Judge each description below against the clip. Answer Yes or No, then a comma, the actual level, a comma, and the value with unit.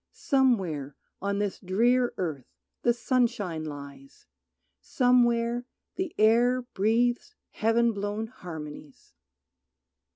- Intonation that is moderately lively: No, wide, 5.8 semitones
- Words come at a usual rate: No, slow, 90 wpm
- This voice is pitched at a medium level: No, high, 220 Hz